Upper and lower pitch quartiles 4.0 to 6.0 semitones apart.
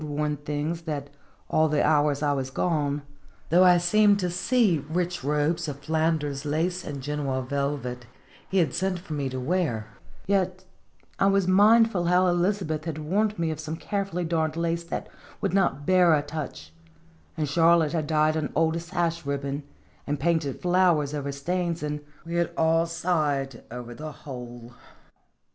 No: average, 3.3 semitones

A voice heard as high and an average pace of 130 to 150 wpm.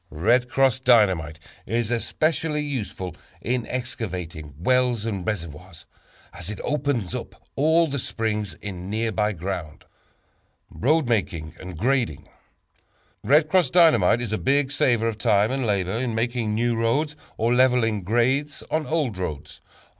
No: low, 115 Hz; average, 140 wpm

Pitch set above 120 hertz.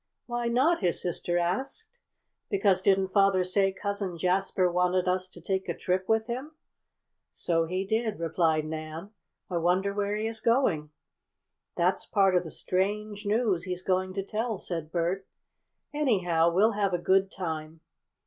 Yes: high, 190 Hz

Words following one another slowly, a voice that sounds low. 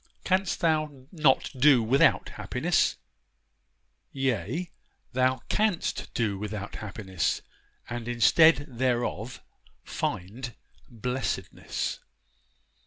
Yes: slow, 80 wpm; low, 125 Hz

